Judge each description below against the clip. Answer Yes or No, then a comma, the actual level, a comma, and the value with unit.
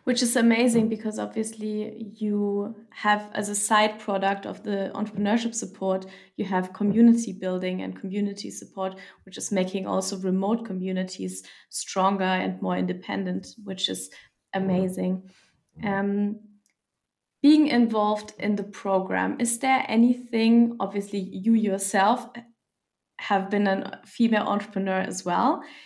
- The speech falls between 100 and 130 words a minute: Yes, slow, 125 wpm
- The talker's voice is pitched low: No, high, 205 Hz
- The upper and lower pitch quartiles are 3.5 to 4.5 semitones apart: No, narrow, 2.6 semitones